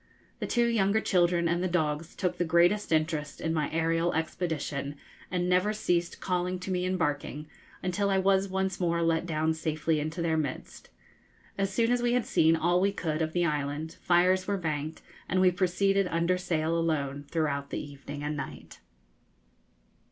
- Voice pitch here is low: No, medium, 170 Hz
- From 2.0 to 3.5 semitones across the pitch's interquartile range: Yes, average, 2.9 semitones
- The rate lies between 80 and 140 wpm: No, average, 180 wpm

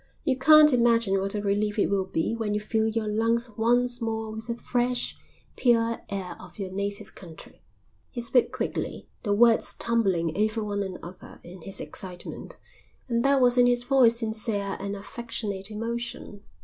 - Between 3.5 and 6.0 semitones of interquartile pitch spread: No, average, 2.9 semitones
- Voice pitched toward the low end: No, high, 220 Hz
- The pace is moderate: Yes, average, 170 wpm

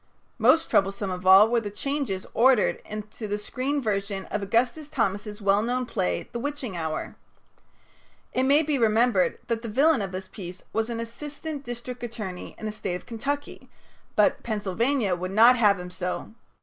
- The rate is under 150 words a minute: No, average, 175 wpm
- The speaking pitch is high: Yes, high, 220 Hz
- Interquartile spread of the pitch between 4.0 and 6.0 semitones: Yes, average, 4.4 semitones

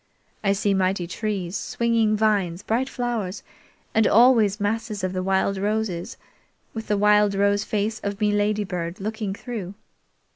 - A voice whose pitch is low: No, high, 205 Hz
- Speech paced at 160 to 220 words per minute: No, average, 145 wpm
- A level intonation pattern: Yes, narrow, 2.2 semitones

